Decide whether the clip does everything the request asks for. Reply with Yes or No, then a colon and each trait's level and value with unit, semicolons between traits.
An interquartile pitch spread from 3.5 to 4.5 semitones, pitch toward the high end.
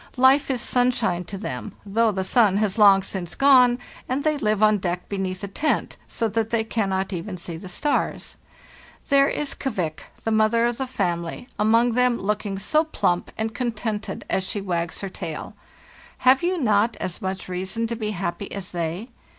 Yes: average, 4.2 semitones; high, 215 Hz